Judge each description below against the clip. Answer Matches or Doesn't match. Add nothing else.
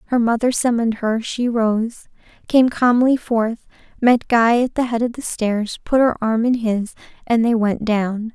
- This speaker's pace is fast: Doesn't match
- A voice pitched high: Matches